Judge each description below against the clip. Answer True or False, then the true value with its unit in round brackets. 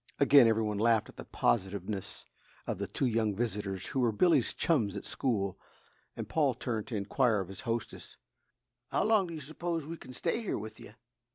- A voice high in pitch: False (115 Hz)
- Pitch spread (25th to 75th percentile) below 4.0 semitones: False (5.5 semitones)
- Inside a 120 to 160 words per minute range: False (195 wpm)